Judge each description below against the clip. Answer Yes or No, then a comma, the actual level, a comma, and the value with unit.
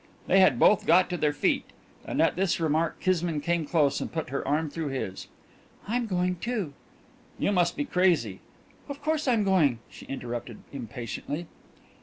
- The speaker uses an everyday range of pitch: Yes, average, 4.8 semitones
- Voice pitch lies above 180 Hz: No, medium, 165 Hz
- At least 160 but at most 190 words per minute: Yes, average, 175 wpm